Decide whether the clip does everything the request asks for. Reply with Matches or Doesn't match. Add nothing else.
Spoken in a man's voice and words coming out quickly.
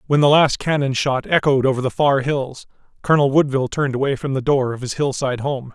Matches